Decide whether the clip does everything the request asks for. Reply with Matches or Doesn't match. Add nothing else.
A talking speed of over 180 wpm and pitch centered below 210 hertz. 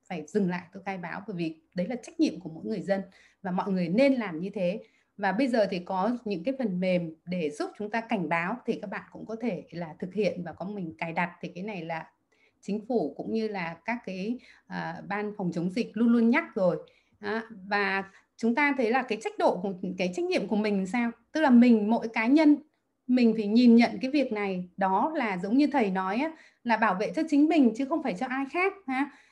Doesn't match